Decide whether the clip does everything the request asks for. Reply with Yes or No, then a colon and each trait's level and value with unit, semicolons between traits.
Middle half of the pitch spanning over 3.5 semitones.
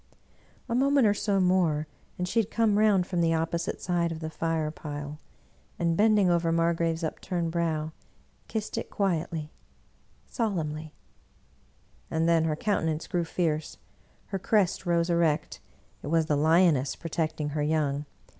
No: average, 2.8 semitones